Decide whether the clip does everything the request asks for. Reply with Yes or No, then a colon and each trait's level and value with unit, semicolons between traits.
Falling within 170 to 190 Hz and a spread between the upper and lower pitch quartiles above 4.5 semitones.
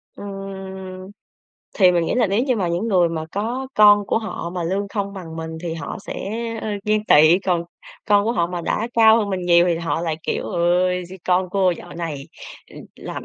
No: medium, 185 Hz; average, 3.2 semitones